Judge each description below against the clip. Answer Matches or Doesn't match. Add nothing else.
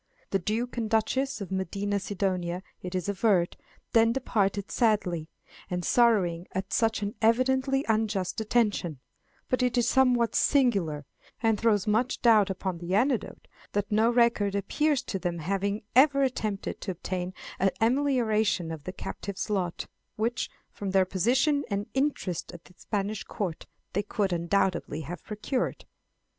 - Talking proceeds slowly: Doesn't match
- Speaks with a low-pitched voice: Doesn't match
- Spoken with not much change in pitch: Doesn't match